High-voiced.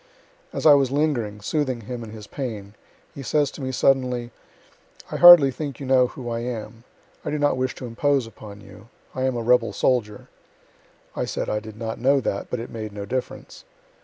No: low, 125 Hz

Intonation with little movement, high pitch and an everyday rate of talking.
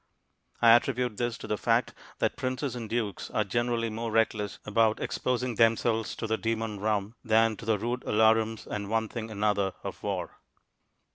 No: narrow, 1.6 semitones; low, 115 Hz; average, 170 wpm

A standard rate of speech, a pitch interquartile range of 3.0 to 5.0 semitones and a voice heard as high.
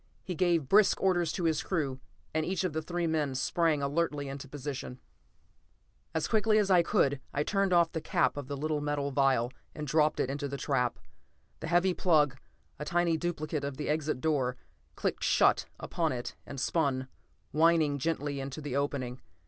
No: average, 180 wpm; average, 3.3 semitones; medium, 150 Hz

